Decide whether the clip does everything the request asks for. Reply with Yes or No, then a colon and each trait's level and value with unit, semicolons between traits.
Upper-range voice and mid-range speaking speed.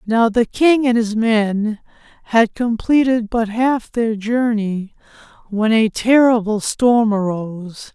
No: high, 225 Hz; slow, 130 wpm